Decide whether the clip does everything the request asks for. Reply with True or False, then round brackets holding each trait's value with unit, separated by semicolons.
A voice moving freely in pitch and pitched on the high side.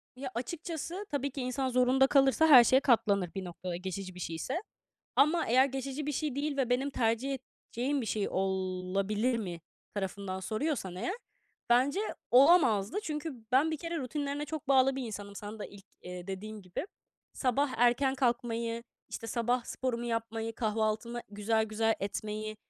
False (4.6 semitones; 240 Hz)